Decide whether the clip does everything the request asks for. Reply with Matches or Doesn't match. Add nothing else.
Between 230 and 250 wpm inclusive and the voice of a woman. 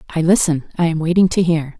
Doesn't match